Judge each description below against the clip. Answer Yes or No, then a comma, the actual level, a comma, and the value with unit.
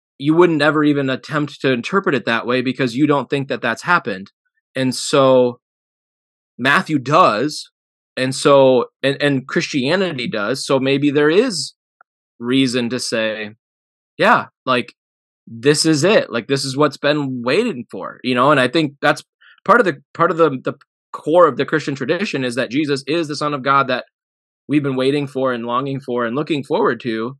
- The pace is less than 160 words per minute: No, average, 185 wpm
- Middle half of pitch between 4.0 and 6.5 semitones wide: No, average, 3.0 semitones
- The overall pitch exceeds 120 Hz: Yes, low, 135 Hz